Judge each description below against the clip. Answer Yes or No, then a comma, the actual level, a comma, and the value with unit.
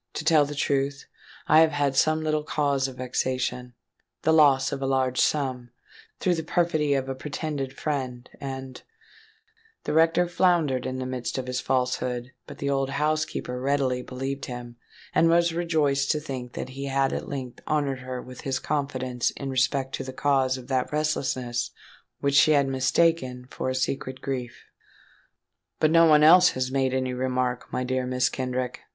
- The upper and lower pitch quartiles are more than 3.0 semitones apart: No, average, 2.7 semitones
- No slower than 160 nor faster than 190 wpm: Yes, average, 170 wpm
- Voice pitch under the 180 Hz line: Yes, low, 135 Hz